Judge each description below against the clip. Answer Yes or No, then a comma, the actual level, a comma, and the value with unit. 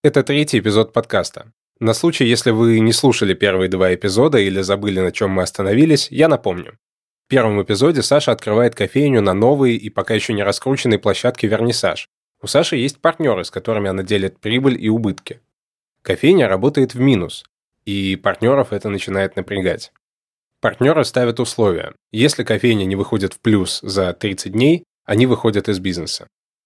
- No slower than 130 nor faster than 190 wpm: Yes, fast, 160 wpm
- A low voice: Yes, low, 110 Hz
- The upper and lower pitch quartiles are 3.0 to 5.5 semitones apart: Yes, average, 4.1 semitones